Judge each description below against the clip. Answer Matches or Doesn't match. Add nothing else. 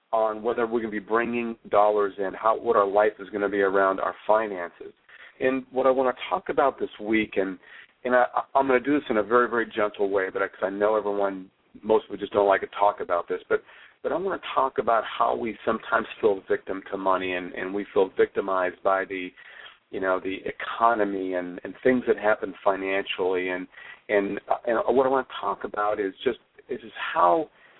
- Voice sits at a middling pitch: Doesn't match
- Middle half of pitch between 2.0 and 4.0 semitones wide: Matches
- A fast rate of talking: Matches